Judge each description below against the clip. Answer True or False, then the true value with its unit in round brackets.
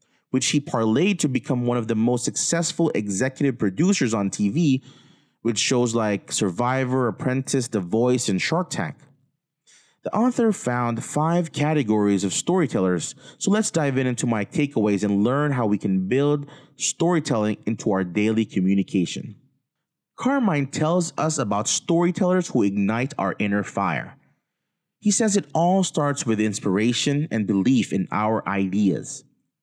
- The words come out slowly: False (145 wpm)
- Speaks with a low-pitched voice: True (130 Hz)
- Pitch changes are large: True (6.6 semitones)